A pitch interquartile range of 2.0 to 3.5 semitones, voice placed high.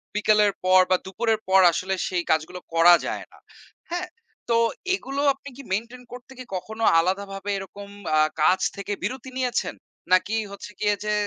No: average, 3.9 semitones; high, 205 Hz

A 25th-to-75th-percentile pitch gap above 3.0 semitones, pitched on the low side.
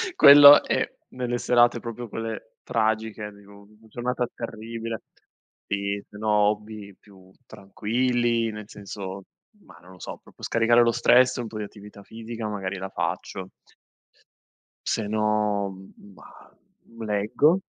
No: narrow, 2.6 semitones; low, 110 Hz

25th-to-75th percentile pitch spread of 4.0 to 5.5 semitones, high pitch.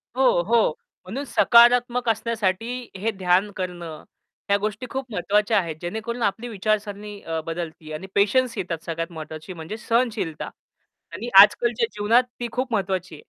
Yes: average, 4.8 semitones; high, 210 Hz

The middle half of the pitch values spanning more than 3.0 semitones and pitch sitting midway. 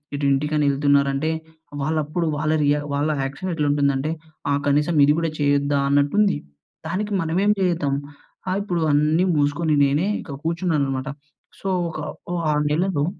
No: average, 2.7 semitones; medium, 150 Hz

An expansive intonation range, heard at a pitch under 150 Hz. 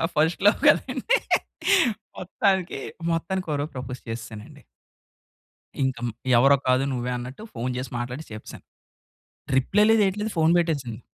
Yes: wide, 7.1 semitones; medium, 140 Hz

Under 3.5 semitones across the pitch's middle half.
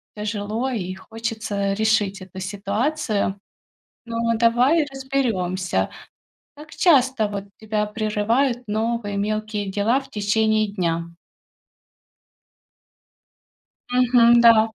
Yes: average, 2.8 semitones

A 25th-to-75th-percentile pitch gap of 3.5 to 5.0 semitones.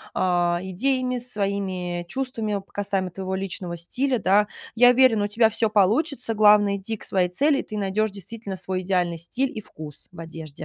Yes: average, 3.8 semitones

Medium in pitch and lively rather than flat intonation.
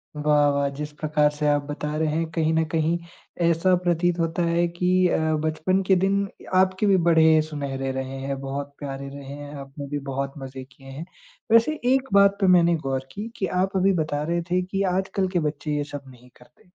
No: medium, 155 Hz; average, 4.1 semitones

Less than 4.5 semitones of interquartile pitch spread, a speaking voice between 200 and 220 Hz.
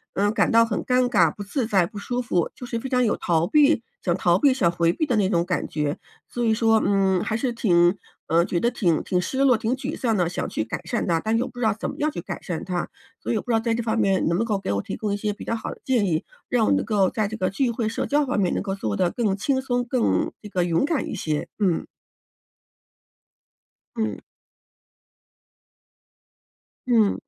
No: average, 5.0 semitones; high, 215 Hz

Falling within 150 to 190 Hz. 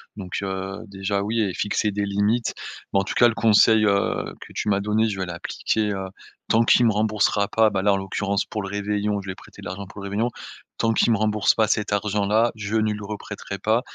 No: low, 105 Hz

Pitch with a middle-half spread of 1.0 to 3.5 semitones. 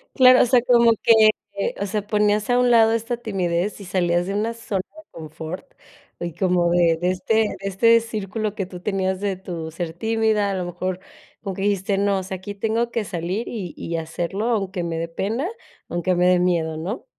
No: average, 3.9 semitones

